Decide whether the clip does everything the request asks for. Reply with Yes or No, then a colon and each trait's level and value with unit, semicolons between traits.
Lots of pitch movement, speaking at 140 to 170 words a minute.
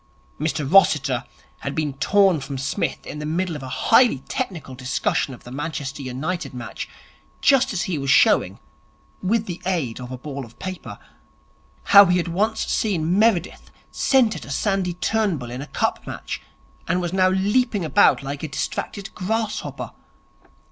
Yes: wide, 6.0 semitones; average, 160 wpm